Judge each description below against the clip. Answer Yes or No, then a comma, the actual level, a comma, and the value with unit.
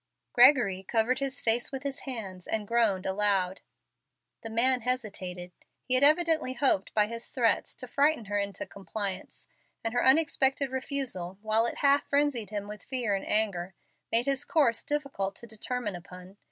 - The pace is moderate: Yes, average, 165 wpm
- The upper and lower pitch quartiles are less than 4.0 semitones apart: No, average, 4.8 semitones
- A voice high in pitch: Yes, high, 230 Hz